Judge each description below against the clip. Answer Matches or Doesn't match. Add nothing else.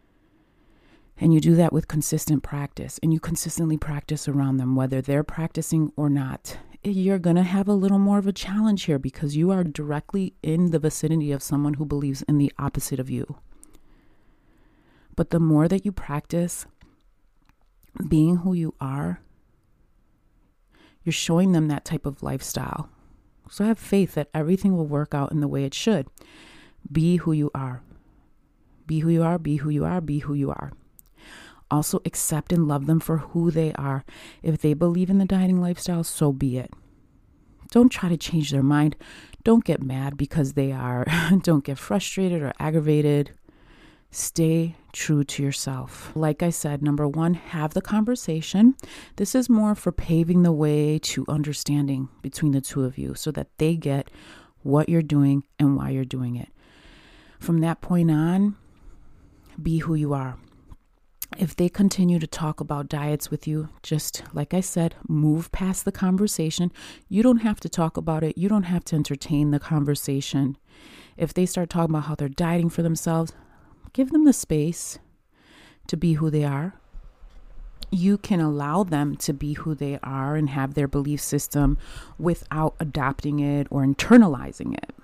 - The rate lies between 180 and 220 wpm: Doesn't match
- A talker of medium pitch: Matches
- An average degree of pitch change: Matches